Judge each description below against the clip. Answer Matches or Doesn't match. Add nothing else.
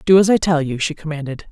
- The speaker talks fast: Matches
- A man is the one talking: Doesn't match